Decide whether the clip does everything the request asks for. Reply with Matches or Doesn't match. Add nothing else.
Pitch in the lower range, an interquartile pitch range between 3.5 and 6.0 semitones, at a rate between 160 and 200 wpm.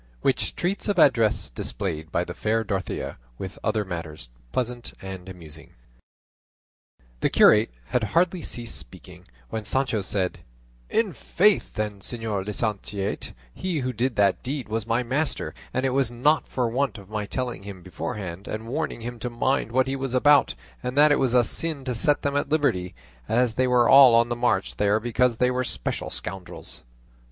Matches